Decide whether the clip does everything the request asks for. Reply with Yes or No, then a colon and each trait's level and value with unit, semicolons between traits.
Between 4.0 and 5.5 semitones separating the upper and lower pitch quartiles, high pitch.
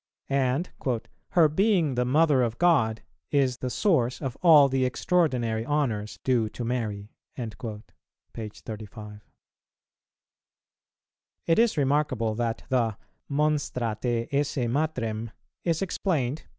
No: average, 4.8 semitones; low, 130 Hz